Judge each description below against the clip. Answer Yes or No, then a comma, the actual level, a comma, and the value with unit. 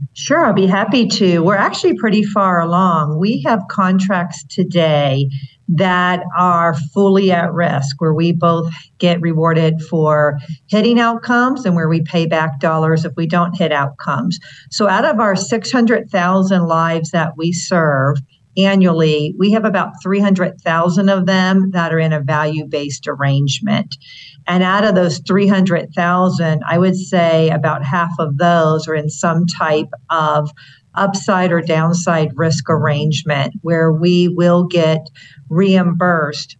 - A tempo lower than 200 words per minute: Yes, average, 145 wpm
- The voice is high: No, medium, 170 Hz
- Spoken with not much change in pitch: No, average, 3.2 semitones